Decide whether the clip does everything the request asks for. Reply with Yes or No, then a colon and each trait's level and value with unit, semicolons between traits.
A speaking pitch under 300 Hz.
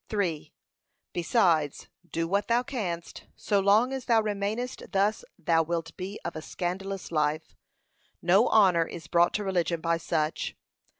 Yes: medium, 185 Hz